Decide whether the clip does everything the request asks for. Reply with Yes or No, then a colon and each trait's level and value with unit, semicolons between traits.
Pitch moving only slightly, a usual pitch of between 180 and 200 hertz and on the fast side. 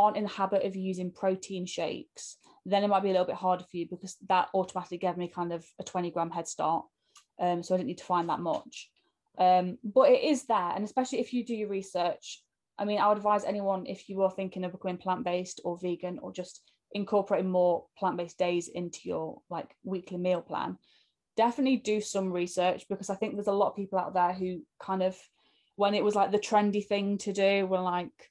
Yes: narrow, 2.1 semitones; high, 190 Hz; fast, 225 wpm